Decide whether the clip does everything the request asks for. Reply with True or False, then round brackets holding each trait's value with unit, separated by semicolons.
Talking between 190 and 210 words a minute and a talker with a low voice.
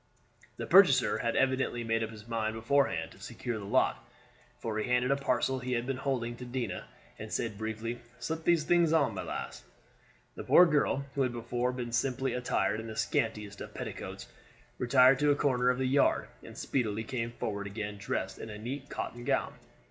True (195 wpm; 120 Hz)